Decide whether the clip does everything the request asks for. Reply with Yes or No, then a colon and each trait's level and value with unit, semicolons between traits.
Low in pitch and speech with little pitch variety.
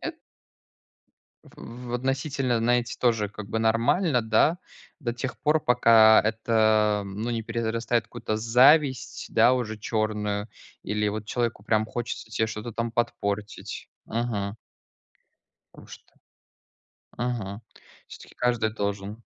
Yes: low, 115 Hz; narrow, 2.1 semitones